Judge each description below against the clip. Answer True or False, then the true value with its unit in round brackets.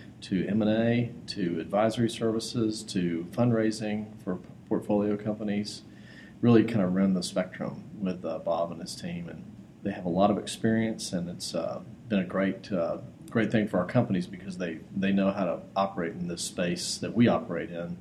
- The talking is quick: False (185 wpm)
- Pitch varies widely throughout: False (3.3 semitones)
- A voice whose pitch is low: True (105 Hz)